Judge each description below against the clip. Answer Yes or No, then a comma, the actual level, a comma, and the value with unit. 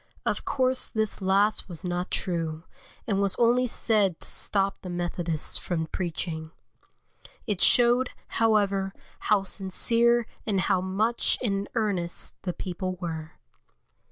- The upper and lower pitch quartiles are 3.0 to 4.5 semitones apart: Yes, average, 3.7 semitones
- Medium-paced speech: No, slow, 130 wpm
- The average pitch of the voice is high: Yes, high, 195 Hz